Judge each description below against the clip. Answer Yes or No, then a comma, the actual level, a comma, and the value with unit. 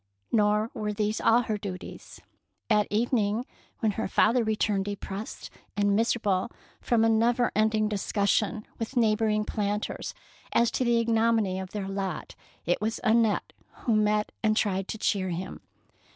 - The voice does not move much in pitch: Yes, narrow, 1.9 semitones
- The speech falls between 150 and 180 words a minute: Yes, average, 155 wpm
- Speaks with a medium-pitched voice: No, high, 215 Hz